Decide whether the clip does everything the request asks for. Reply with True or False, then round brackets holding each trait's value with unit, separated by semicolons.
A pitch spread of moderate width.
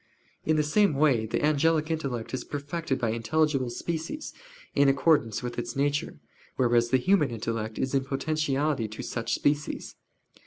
True (4.4 semitones)